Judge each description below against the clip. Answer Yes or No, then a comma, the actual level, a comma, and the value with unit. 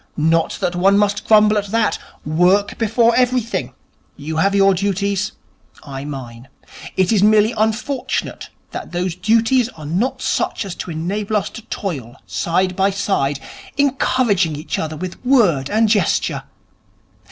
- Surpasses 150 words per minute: No, average, 145 wpm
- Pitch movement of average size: Yes, average, 4.8 semitones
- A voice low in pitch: No, high, 195 Hz